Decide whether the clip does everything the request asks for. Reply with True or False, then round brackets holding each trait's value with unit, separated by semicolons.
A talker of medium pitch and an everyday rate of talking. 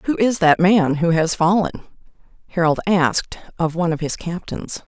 True (175 Hz; 170 wpm)